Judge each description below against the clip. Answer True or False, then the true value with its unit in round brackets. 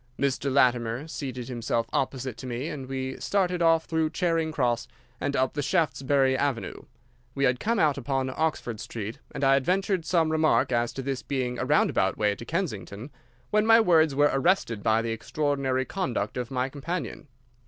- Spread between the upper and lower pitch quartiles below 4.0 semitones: False (4.3 semitones)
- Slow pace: False (180 wpm)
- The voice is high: False (135 Hz)